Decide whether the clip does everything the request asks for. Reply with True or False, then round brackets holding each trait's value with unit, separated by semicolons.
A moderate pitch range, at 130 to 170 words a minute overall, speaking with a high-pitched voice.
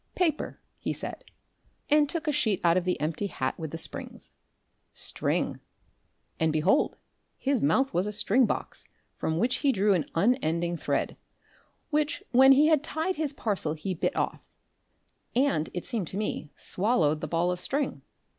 False (8.5 semitones; 165 wpm; 205 Hz)